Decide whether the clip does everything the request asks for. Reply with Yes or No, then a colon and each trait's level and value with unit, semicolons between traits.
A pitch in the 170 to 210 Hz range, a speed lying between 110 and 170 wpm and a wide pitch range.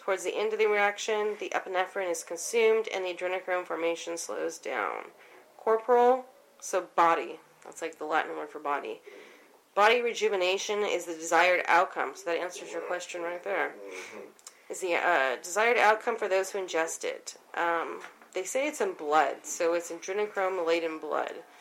Yes: high, 190 Hz; average, 165 wpm; wide, 6.7 semitones